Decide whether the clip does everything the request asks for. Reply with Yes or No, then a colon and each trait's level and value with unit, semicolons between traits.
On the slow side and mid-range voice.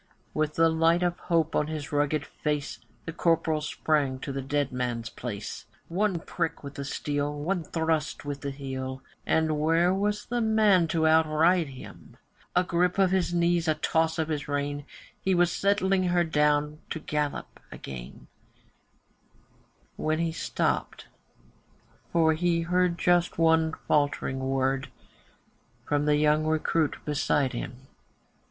No: average, 145 wpm; medium, 155 Hz